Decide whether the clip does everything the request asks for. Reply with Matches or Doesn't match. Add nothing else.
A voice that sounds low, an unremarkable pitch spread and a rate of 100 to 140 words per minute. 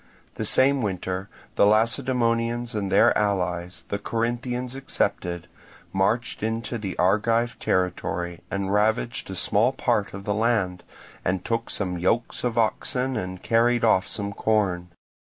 Matches